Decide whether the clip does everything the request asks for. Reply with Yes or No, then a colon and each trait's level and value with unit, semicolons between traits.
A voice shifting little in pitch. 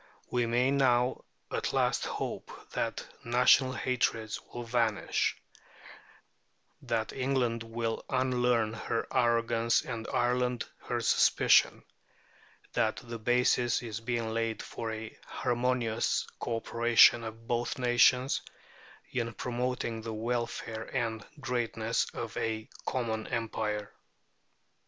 Yes: narrow, 1.5 semitones